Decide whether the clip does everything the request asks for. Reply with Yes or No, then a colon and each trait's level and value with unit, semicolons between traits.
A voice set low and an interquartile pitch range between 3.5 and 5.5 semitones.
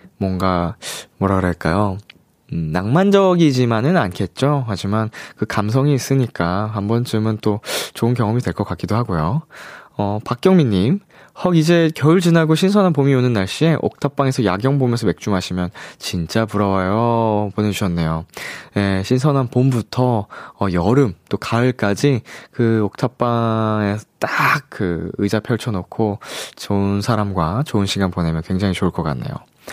Yes: low, 110 Hz; average, 5.2 semitones